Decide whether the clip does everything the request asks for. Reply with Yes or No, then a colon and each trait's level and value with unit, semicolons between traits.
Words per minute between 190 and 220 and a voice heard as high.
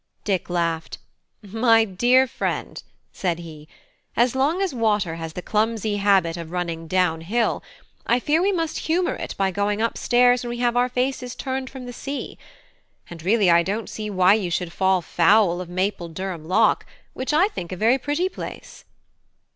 No: average, 180 wpm; high, 210 Hz